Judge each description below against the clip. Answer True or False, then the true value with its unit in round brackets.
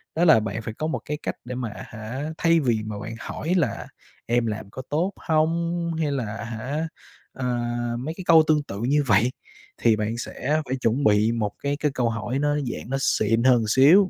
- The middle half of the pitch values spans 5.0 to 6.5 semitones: True (5.3 semitones)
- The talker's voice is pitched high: False (130 Hz)